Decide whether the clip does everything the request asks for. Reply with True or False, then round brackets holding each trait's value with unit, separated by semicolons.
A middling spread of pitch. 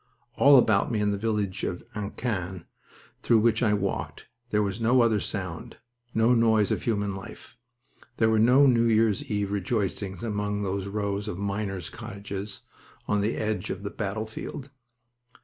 False (2.1 semitones)